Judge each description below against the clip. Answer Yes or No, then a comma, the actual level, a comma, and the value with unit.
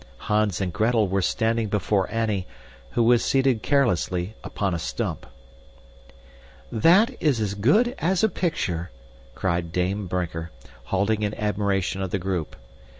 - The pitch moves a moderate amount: Yes, average, 4.0 semitones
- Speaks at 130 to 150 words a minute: Yes, average, 140 wpm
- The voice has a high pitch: No, low, 105 Hz